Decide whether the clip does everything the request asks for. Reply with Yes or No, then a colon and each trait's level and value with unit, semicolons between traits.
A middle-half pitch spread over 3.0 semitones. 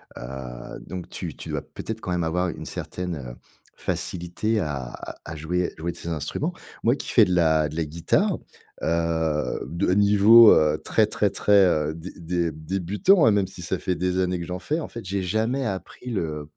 Yes: average, 3.9 semitones